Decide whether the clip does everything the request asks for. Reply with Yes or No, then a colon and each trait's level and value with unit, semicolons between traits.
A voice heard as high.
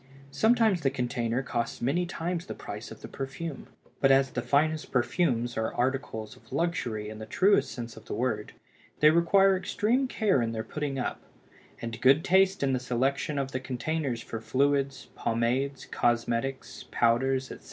No: low, 135 Hz